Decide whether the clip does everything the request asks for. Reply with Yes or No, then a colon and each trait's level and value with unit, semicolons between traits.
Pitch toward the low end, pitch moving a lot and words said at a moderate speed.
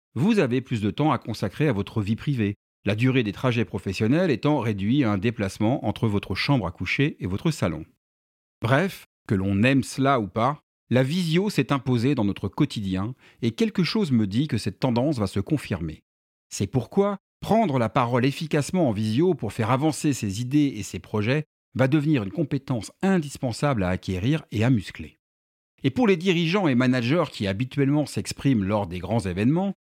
Yes: low, 125 Hz; wide, 6.3 semitones; average, 185 wpm